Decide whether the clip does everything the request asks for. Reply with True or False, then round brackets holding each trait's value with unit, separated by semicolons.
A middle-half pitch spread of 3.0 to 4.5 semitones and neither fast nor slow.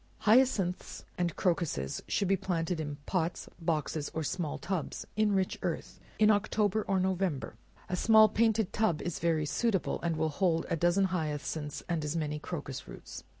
True (3.8 semitones; 165 wpm)